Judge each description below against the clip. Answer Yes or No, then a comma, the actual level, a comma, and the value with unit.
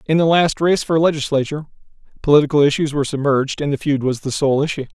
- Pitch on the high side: No, medium, 145 Hz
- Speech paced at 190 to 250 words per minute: Yes, fast, 205 wpm